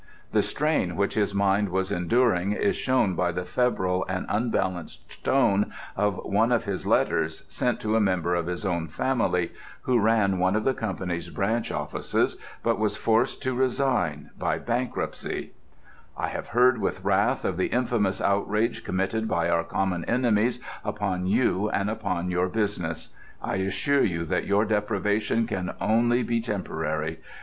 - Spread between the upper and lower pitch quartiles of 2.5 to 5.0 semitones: Yes, average, 4.1 semitones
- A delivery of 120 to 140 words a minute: No, average, 160 wpm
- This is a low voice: Yes, low, 100 Hz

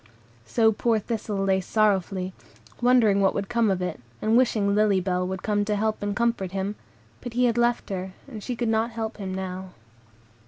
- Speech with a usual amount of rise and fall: Yes, average, 3.1 semitones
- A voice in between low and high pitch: No, high, 210 Hz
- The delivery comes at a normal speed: Yes, average, 195 wpm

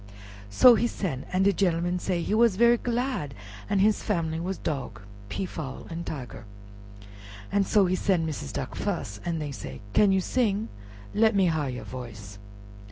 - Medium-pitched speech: Yes, medium, 175 Hz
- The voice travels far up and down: Yes, wide, 6.1 semitones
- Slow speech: No, average, 165 wpm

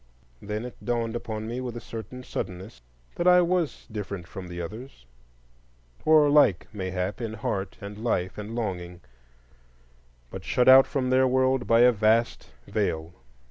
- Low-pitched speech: Yes, low, 115 Hz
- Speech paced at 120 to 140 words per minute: No, average, 155 wpm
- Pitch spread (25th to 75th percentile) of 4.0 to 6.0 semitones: Yes, average, 4.7 semitones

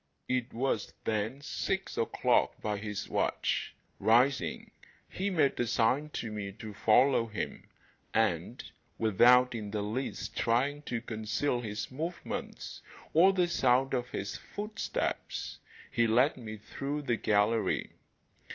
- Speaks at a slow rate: Yes, slow, 130 wpm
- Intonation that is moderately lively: Yes, average, 4.0 semitones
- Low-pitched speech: Yes, low, 120 Hz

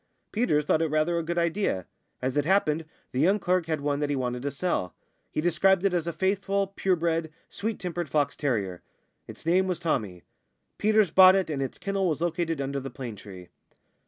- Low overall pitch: No, medium, 165 Hz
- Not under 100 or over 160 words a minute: No, fast, 205 wpm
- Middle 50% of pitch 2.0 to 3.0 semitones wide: No, average, 4.8 semitones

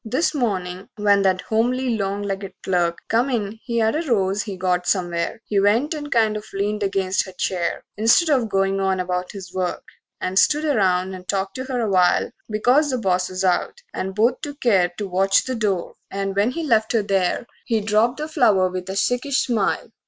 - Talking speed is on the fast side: Yes, fast, 210 wpm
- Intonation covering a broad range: No, average, 4.0 semitones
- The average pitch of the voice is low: No, high, 205 Hz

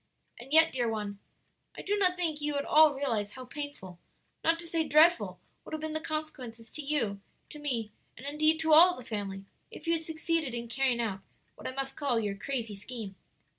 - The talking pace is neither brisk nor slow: No, fast, 210 wpm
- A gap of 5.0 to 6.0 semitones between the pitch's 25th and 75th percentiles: Yes, wide, 5.5 semitones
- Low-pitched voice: No, very high, 275 Hz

